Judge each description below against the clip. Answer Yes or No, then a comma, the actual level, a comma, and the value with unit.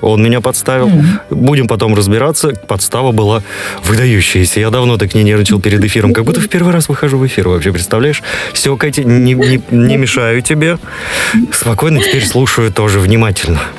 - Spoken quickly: Yes, fast, 165 wpm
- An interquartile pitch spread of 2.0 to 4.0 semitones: No, average, 4.4 semitones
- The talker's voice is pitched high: No, low, 120 Hz